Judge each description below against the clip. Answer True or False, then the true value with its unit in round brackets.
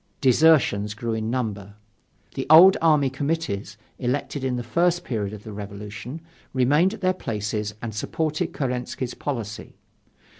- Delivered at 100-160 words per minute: True (140 wpm)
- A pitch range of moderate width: False (6.1 semitones)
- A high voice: False (125 Hz)